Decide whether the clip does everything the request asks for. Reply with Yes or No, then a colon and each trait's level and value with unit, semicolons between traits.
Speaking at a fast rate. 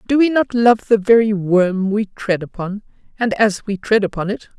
Yes: fast, 210 wpm